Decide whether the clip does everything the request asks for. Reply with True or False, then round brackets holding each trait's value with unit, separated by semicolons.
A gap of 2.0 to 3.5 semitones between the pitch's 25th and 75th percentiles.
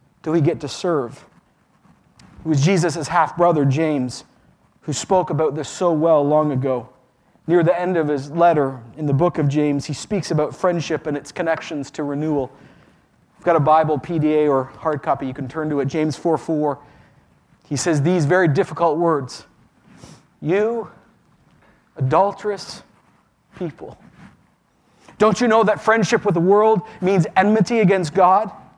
False (3.9 semitones)